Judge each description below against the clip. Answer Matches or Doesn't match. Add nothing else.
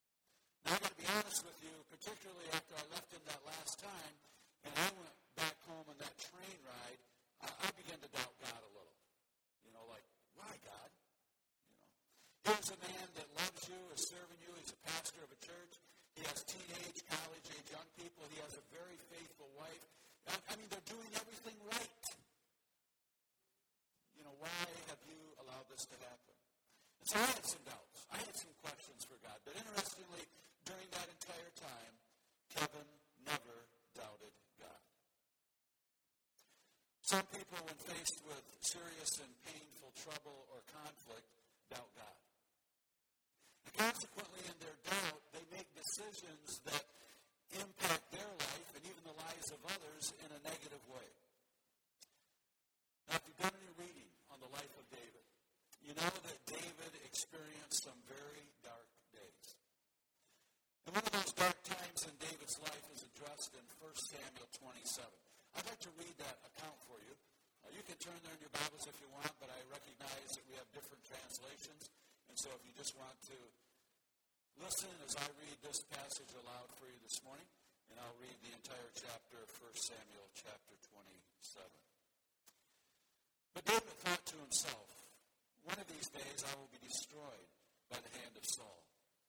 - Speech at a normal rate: Matches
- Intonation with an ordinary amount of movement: Matches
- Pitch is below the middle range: Doesn't match